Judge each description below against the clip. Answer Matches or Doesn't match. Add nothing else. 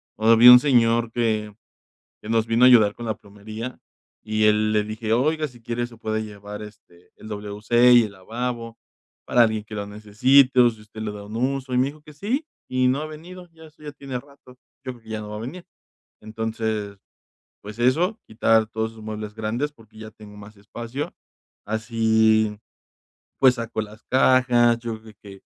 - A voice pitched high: Doesn't match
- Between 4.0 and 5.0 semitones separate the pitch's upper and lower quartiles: Doesn't match